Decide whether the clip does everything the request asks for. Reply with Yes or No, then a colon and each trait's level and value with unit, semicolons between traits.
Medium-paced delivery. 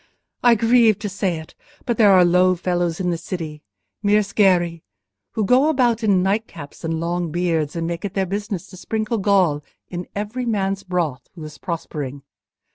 Yes: average, 175 wpm